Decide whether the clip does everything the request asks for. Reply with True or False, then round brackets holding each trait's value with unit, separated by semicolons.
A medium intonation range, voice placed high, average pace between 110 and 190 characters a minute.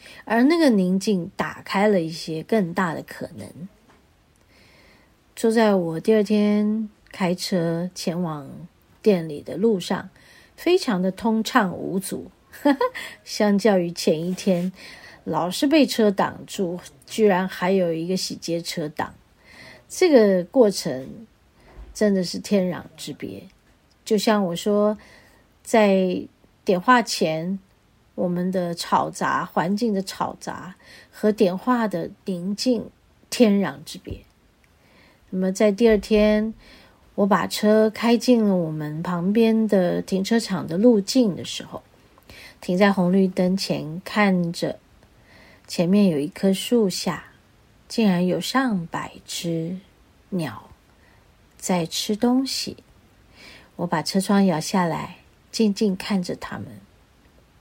True (3.8 semitones; 195 Hz; 170 characters per minute)